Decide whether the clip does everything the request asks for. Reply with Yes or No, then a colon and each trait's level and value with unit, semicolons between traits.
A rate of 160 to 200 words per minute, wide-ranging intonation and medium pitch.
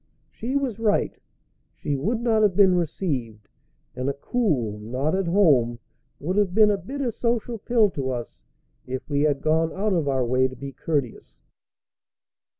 Yes: average, 165 wpm; wide, 8.2 semitones; medium, 160 Hz